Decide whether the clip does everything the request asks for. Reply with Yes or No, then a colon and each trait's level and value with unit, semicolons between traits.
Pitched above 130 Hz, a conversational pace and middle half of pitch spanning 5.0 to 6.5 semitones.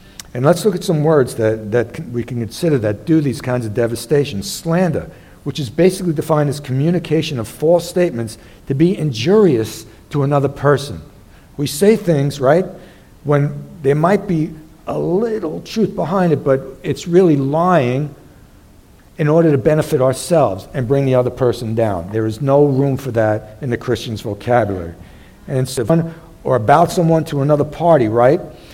Yes: medium, 140 Hz; average, 165 wpm; wide, 5.5 semitones